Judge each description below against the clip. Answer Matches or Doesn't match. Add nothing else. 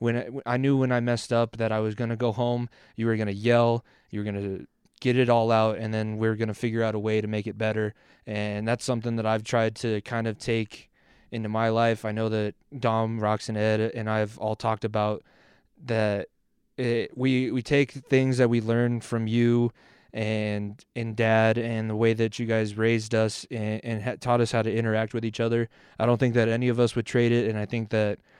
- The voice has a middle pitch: Doesn't match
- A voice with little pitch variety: Matches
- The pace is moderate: Doesn't match